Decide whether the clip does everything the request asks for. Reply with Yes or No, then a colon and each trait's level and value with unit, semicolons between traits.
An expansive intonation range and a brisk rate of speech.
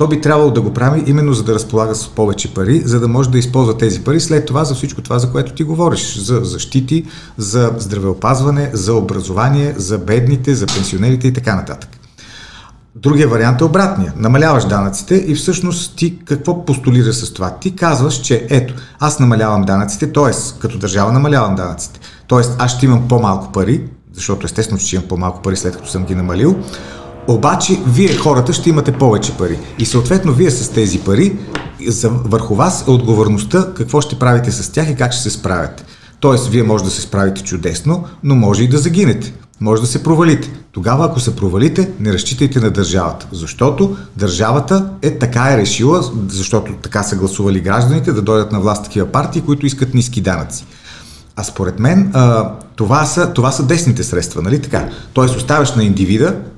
Yes: wide, 5.7 semitones; fast, 180 wpm